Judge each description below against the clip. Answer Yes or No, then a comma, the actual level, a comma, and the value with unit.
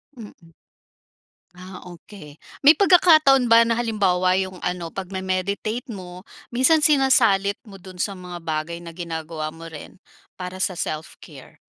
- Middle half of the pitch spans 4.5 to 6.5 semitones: Yes, average, 4.8 semitones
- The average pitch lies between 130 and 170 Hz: No, medium, 185 Hz